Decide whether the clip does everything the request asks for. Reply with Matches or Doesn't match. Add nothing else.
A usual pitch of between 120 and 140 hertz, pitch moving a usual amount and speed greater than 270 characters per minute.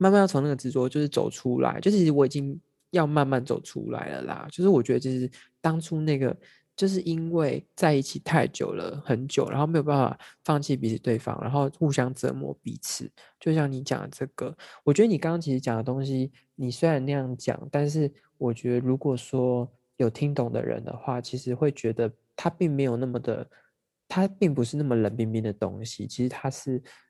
Matches